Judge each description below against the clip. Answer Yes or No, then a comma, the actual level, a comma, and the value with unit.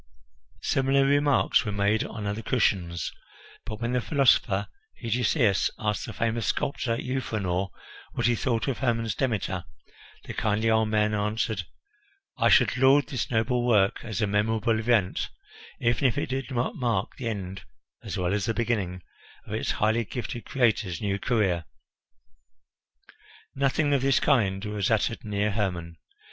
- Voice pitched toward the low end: Yes, low, 110 Hz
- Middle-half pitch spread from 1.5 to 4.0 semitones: Yes, average, 3.4 semitones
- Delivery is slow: No, average, 150 wpm